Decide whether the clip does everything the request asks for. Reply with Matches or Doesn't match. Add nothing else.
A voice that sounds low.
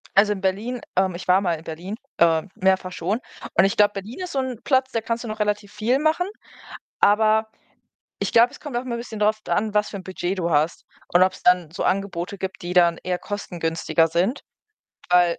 Doesn't match